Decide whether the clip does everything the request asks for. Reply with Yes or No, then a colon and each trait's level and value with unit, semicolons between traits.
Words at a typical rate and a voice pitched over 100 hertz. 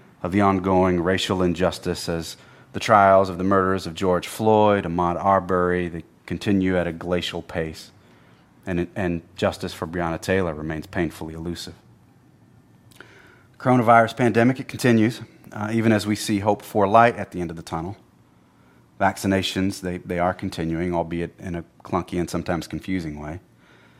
No: average, 155 wpm; very low, 90 Hz